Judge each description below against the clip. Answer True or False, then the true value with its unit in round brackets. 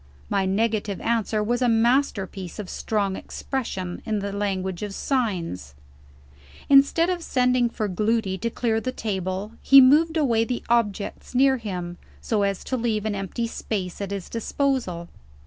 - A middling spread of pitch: True (4.0 semitones)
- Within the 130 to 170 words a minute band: True (155 wpm)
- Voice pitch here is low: False (215 Hz)